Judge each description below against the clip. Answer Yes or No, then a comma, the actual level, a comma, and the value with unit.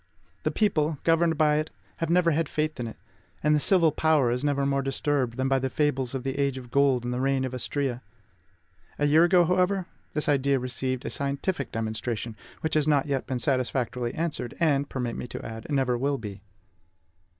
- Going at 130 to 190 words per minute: No, average, 200 wpm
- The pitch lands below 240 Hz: Yes, medium, 140 Hz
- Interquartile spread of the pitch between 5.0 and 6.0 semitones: No, average, 3.4 semitones